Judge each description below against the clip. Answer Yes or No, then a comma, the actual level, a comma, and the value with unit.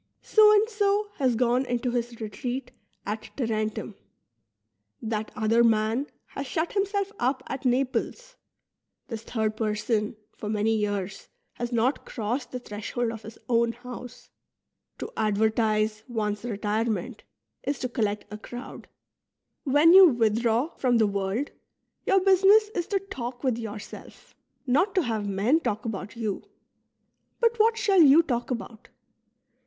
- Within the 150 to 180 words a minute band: No, average, 140 wpm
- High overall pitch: Yes, high, 240 Hz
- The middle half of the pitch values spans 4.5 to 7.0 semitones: Yes, average, 4.8 semitones